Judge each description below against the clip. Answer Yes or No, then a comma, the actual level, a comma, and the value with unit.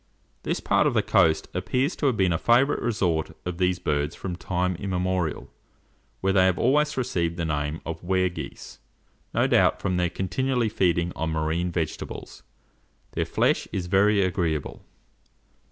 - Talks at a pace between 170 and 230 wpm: No, average, 160 wpm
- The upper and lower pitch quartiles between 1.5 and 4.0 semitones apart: Yes, average, 2.9 semitones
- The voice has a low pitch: Yes, very low, 90 Hz